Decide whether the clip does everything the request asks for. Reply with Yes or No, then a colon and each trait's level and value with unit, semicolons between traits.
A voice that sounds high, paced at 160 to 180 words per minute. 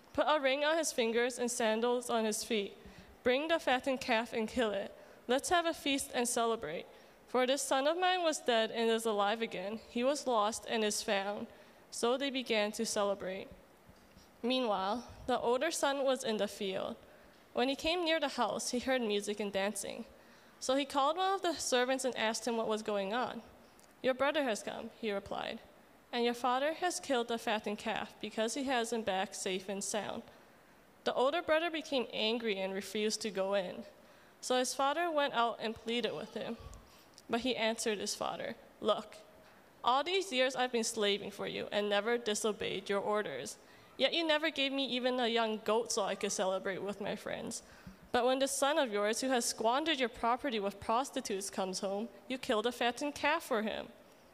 No: high, 235 Hz; average, 195 wpm